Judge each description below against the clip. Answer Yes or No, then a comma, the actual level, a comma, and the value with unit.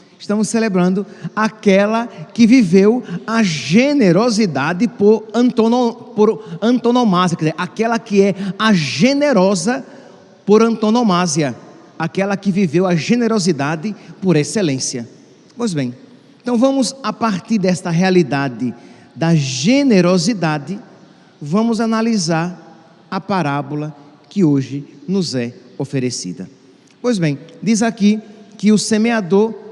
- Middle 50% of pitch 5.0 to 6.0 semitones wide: Yes, wide, 5.5 semitones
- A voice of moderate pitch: No, high, 195 Hz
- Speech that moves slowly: Yes, slow, 105 wpm